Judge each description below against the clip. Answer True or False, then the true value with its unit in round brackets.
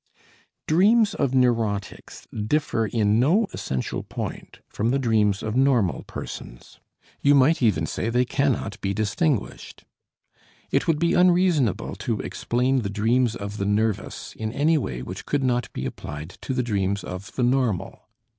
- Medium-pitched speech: False (120 Hz)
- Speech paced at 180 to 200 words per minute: False (155 wpm)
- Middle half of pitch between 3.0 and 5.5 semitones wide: True (5.1 semitones)